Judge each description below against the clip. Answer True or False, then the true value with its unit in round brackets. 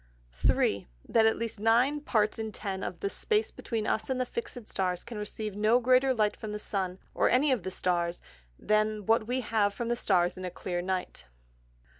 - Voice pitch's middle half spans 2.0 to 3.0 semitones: False (4.1 semitones)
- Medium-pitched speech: False (215 Hz)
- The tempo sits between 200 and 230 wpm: True (205 wpm)